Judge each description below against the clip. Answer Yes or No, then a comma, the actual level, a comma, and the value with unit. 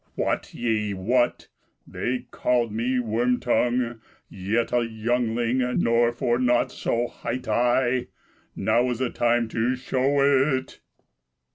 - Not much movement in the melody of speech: Yes, narrow, 1.4 semitones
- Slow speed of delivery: Yes, slow, 120 wpm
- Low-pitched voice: Yes, low, 120 Hz